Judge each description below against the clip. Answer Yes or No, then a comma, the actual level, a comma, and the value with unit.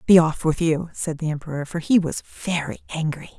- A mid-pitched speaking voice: Yes, medium, 160 Hz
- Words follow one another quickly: Yes, fast, 210 wpm